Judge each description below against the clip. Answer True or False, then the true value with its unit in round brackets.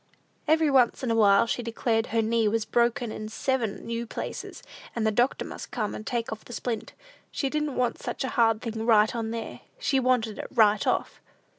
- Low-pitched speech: False (230 Hz)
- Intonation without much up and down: True (2.1 semitones)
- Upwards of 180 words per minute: True (205 wpm)